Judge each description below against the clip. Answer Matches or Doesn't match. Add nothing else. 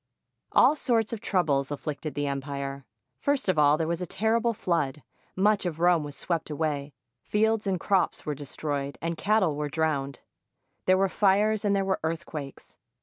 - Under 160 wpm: Doesn't match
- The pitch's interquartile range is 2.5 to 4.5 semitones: Doesn't match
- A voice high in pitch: Doesn't match